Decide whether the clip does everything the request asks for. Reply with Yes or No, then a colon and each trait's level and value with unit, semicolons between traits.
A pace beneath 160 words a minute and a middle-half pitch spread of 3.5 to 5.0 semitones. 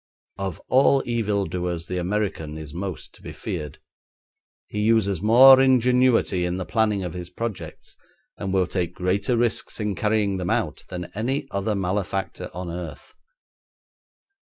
Yes: average, 150 wpm; average, 3.8 semitones